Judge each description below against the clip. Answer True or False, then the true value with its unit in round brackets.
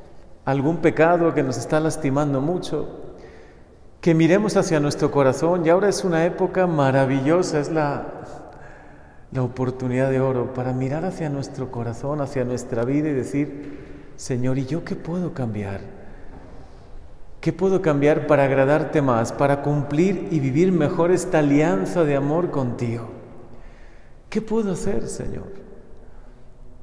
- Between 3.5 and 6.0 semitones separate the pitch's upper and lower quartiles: True (4.1 semitones)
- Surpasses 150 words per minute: False (135 wpm)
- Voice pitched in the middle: True (150 Hz)